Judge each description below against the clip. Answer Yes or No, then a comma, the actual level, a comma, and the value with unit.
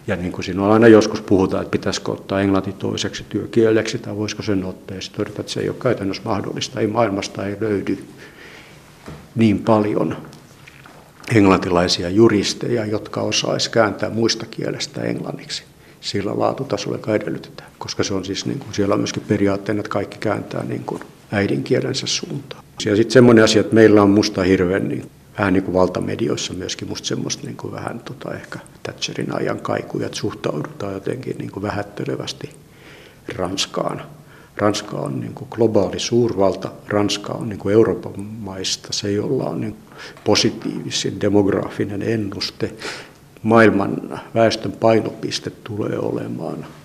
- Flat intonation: Yes, narrow, 2.3 semitones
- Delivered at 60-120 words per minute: No, average, 145 wpm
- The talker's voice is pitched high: No, low, 105 Hz